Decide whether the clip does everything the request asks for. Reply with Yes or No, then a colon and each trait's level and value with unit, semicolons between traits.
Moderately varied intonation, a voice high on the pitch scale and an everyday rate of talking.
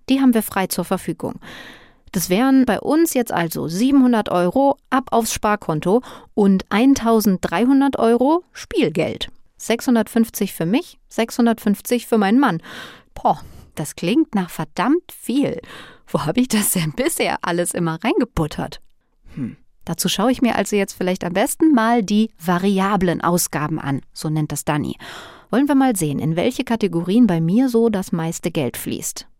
No: wide, 6.0 semitones; high, 215 Hz; average, 155 wpm